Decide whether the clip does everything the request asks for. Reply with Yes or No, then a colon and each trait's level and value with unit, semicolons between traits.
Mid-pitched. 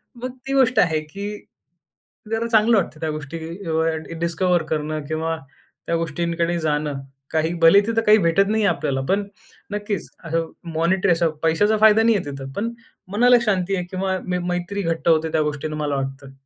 Yes: medium, 170 Hz